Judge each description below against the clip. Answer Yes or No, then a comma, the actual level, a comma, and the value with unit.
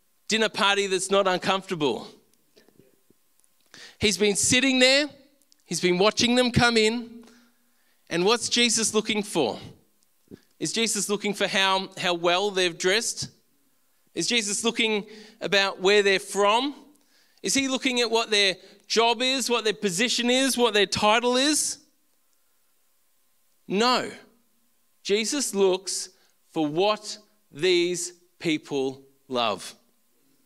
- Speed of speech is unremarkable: No, slow, 120 wpm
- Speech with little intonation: No, average, 4.1 semitones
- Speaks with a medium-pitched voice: No, high, 215 Hz